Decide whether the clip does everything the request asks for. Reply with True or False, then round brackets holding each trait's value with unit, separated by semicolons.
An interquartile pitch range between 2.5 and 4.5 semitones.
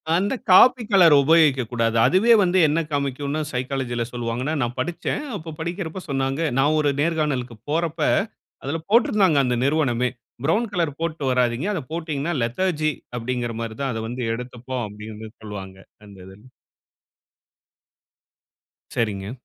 False (5.5 semitones)